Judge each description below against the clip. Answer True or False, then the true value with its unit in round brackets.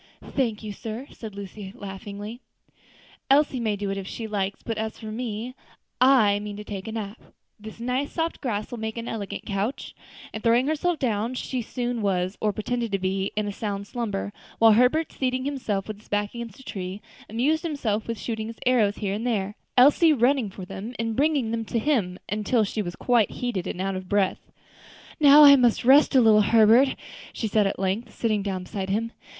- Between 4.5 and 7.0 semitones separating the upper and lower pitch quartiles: False (3.4 semitones)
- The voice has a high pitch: True (220 Hz)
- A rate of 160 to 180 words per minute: False (200 wpm)